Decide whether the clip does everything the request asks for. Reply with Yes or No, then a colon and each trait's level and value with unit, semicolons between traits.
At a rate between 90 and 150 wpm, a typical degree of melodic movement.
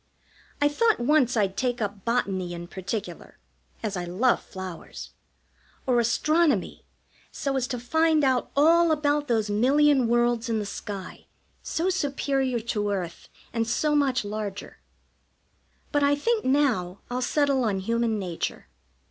No: average, 140 wpm; wide, 5.7 semitones